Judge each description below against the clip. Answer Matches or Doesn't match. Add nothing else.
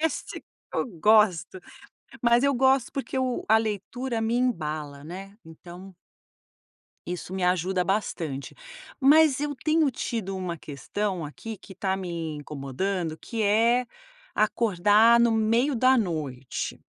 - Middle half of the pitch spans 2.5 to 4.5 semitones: Doesn't match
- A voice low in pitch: Doesn't match